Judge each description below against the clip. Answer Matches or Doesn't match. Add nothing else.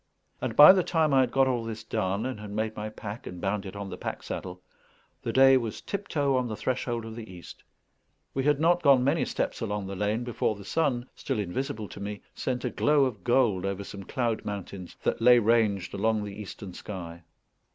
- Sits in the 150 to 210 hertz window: Doesn't match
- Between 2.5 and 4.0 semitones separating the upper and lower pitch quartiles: Doesn't match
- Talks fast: Matches